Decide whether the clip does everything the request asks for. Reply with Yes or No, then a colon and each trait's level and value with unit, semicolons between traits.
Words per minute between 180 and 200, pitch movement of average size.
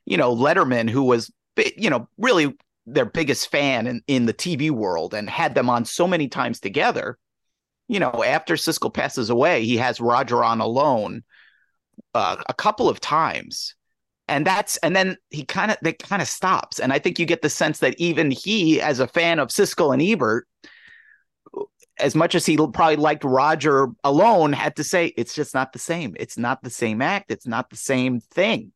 Yes: average, 195 wpm; average, 4.7 semitones